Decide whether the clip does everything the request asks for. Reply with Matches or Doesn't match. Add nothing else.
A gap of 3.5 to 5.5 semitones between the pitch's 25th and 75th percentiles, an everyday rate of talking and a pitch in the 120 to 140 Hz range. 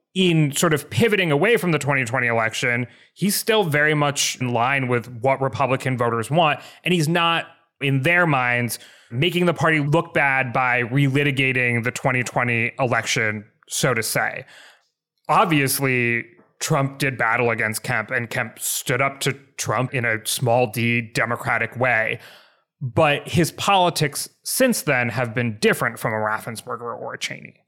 Matches